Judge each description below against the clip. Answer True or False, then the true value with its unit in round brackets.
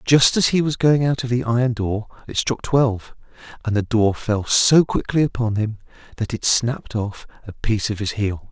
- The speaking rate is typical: False (210 wpm)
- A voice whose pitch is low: True (115 Hz)